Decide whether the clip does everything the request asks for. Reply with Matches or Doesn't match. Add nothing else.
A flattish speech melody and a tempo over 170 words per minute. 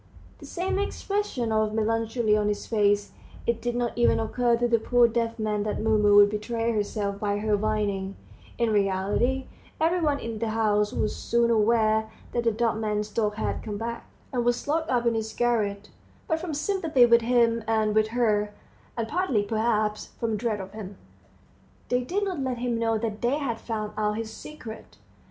Matches